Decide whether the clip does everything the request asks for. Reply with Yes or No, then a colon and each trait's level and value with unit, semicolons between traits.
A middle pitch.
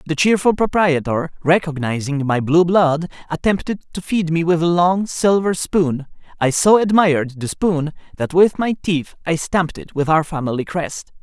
Yes: medium, 165 Hz